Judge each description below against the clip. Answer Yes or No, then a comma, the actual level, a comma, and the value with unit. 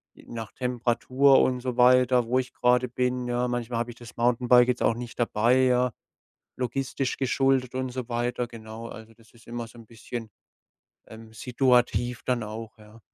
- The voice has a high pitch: No, low, 120 Hz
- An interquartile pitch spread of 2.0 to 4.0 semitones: No, narrow, 1.5 semitones